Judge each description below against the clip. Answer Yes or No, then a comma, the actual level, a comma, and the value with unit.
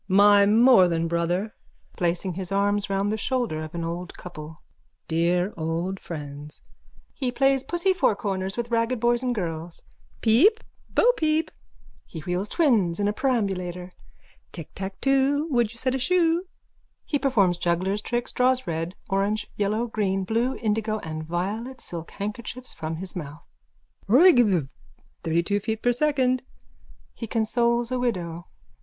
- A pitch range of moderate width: No, wide, 5.8 semitones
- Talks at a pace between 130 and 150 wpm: Yes, slow, 135 wpm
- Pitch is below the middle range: No, high, 205 Hz